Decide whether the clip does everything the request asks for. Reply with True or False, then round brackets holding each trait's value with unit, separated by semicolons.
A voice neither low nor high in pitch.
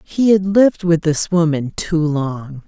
True (170 Hz)